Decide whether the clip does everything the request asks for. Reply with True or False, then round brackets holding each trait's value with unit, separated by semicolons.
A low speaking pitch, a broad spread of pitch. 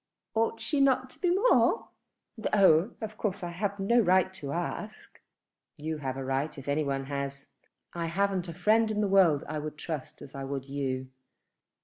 False (170 Hz; 6.9 semitones)